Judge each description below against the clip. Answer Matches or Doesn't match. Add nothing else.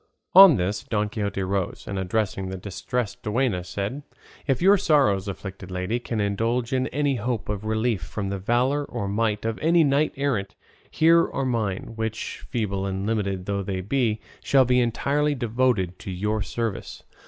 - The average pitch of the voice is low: Matches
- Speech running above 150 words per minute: Matches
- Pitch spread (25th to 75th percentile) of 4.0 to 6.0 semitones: Matches